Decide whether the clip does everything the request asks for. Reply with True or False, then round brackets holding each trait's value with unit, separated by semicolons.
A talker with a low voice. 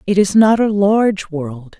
False (190 Hz)